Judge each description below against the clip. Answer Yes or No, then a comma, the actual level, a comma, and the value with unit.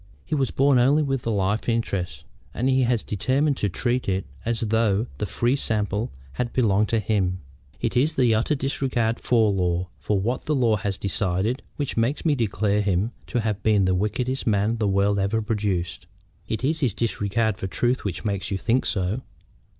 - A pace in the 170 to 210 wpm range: Yes, average, 190 wpm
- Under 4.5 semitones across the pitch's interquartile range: Yes, average, 3.9 semitones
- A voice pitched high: No, low, 110 Hz